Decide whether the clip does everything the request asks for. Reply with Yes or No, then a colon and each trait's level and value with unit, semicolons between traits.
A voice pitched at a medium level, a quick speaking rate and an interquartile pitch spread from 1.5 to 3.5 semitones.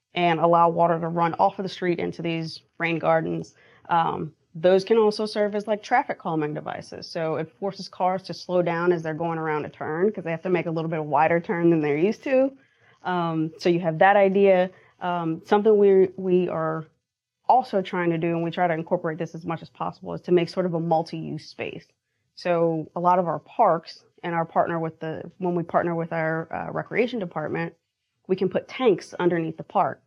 Yes: medium, 170 Hz; fast, 220 wpm; narrow, 2.5 semitones